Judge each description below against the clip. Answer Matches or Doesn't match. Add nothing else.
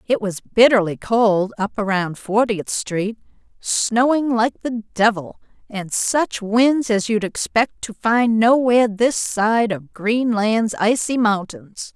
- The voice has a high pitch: Matches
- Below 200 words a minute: Matches